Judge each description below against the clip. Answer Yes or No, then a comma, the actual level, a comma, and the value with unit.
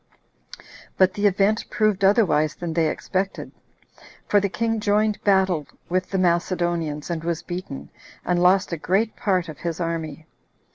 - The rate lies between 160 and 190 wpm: No, average, 150 wpm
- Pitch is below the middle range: No, medium, 185 Hz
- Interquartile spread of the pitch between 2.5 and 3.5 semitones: Yes, average, 3.0 semitones